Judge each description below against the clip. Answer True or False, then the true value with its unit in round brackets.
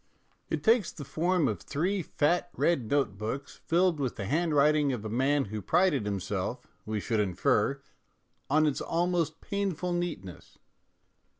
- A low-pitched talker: False (145 Hz)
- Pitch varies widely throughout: True (8.0 semitones)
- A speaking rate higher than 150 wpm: False (145 wpm)